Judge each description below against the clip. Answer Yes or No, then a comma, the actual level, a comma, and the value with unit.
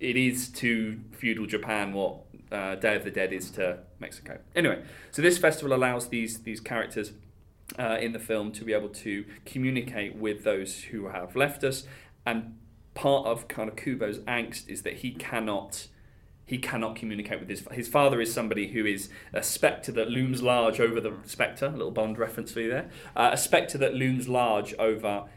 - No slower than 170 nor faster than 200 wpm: Yes, average, 190 wpm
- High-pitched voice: No, low, 115 Hz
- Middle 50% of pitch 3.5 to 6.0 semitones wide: No, average, 2.8 semitones